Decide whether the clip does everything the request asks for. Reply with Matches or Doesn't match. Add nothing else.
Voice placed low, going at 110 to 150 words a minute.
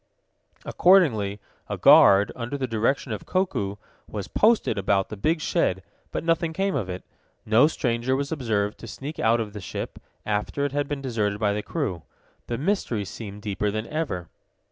Doesn't match